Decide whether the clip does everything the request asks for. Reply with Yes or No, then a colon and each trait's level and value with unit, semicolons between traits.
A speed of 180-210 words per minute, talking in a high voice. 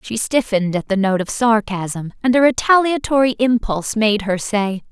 No: average, 170 wpm; high, 220 Hz